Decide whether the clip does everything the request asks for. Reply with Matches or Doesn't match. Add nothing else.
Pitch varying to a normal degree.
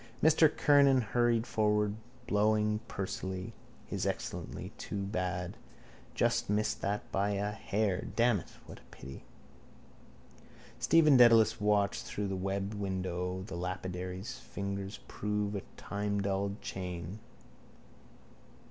Doesn't match